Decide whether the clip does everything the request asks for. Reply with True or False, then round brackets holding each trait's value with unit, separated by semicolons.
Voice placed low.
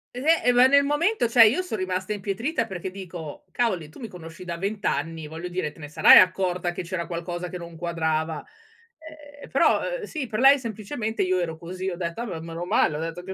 False (185 Hz)